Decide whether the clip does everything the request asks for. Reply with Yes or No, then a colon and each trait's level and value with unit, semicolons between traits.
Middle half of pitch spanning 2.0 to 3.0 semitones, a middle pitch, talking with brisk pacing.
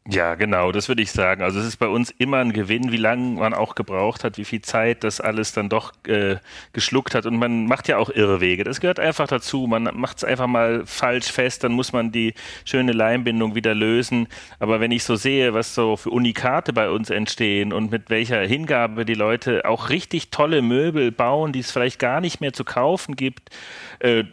No: narrow, 2.4 semitones; low, 115 Hz; fast, 220 wpm